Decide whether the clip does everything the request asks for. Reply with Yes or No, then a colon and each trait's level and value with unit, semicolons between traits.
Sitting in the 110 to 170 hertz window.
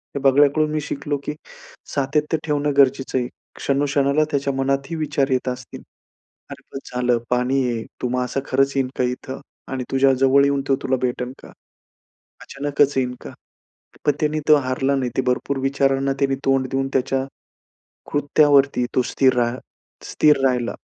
Yes: low, 135 Hz